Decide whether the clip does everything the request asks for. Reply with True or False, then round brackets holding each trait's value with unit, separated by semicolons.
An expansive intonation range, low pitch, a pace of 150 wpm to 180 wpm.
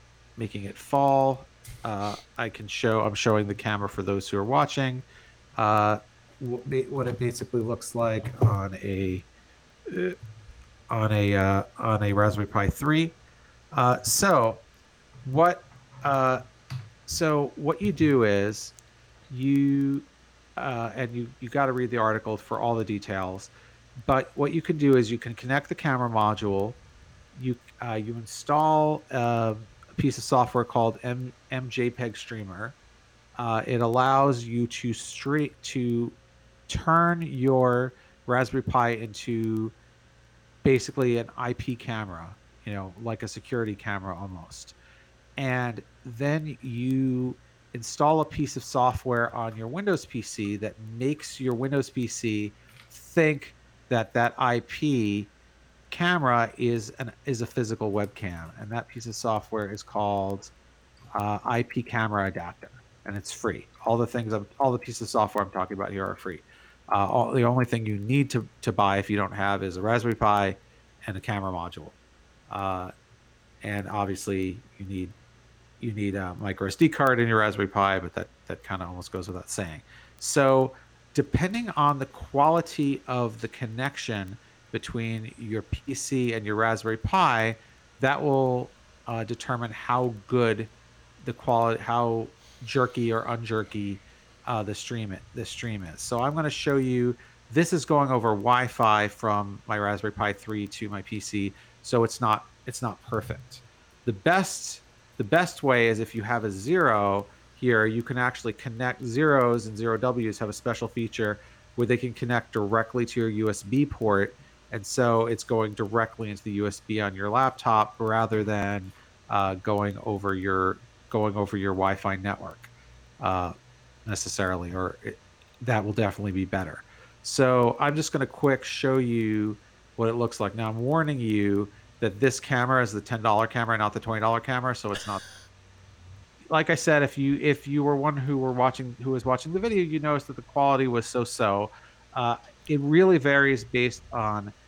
False (3.5 semitones; 115 Hz; 160 wpm)